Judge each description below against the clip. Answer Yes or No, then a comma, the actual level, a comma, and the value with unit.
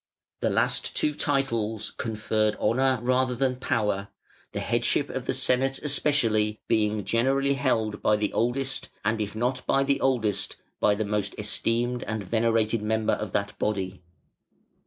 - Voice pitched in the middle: No, low, 110 Hz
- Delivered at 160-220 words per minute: No, average, 150 wpm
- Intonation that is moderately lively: Yes, average, 3.5 semitones